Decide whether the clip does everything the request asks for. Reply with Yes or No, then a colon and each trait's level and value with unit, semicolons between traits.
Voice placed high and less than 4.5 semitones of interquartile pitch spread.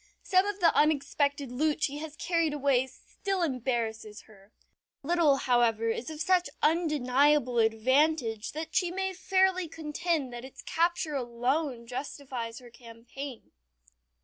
No: very high, 285 Hz; average, 5.0 semitones